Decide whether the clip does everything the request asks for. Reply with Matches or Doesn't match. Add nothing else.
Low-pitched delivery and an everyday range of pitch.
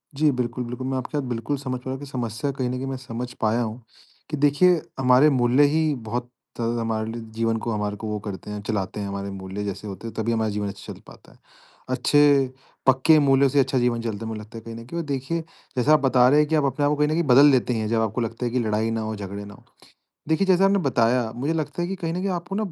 Matches